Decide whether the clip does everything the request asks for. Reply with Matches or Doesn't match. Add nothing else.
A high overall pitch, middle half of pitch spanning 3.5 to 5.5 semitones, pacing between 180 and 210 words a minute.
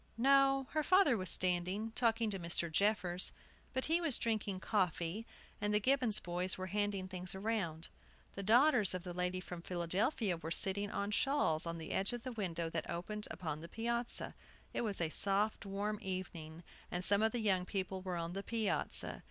Matches